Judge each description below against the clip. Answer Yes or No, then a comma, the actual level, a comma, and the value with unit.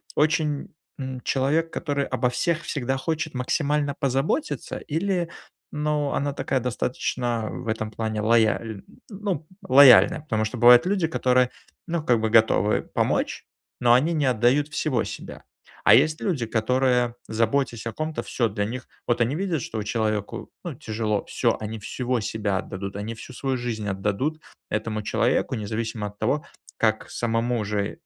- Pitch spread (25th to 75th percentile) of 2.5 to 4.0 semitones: No, average, 4.8 semitones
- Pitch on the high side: No, low, 125 Hz